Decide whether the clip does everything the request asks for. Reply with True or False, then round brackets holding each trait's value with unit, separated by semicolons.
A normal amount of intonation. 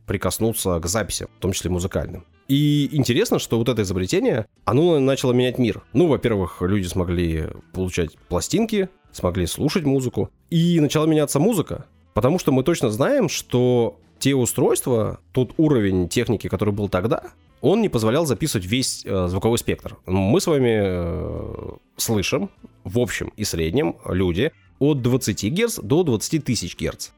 False (6.1 semitones)